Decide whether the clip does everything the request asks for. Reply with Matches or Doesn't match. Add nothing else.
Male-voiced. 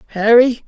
Matches